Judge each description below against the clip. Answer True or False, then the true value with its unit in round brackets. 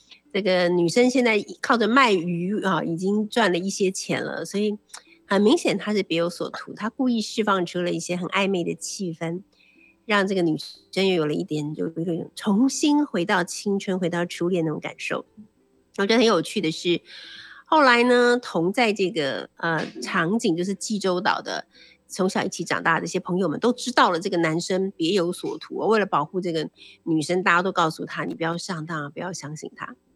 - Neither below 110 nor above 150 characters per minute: False (285 characters per minute)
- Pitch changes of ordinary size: True (3.9 semitones)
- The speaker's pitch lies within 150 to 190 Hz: True (185 Hz)